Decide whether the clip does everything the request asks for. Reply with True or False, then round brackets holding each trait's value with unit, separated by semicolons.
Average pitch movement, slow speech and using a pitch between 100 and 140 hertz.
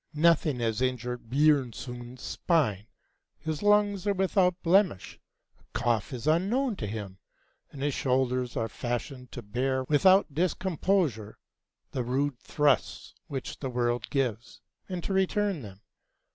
False (6.3 semitones; 130 wpm; 135 Hz)